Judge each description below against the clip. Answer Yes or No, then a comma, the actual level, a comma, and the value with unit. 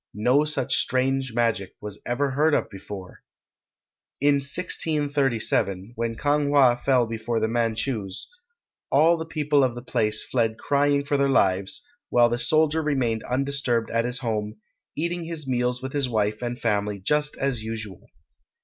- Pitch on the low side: Yes, low, 125 Hz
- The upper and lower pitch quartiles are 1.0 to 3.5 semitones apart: No, average, 4.1 semitones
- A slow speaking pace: No, average, 155 wpm